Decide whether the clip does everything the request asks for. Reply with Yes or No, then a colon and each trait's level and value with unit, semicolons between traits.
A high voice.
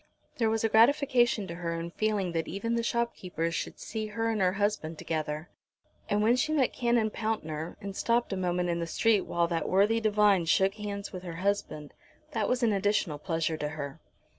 Yes: high, 200 Hz